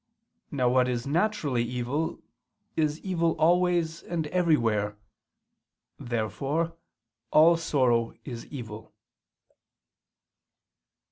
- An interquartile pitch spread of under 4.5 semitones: No, wide, 5.6 semitones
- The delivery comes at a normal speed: No, slow, 80 wpm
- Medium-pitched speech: Yes, medium, 145 Hz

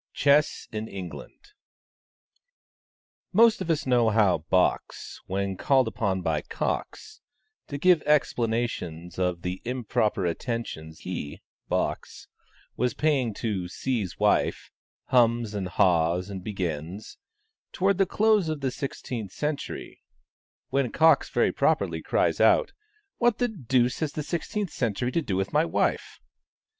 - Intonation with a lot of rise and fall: Yes, wide, 8.0 semitones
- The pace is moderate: No, slow, 130 wpm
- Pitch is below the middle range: Yes, low, 115 Hz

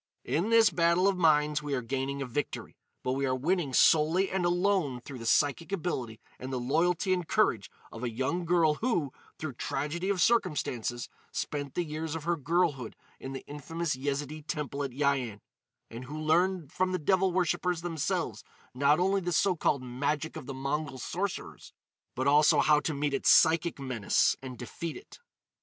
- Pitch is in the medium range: Yes, medium, 150 Hz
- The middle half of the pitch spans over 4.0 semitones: Yes, average, 4.5 semitones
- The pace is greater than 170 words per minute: Yes, average, 180 wpm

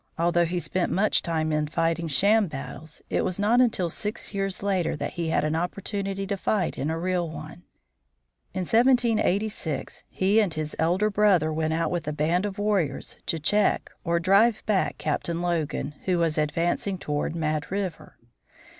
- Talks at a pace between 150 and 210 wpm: Yes, average, 170 wpm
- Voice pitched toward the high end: No, medium, 175 Hz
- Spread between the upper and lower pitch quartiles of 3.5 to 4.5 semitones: Yes, average, 3.9 semitones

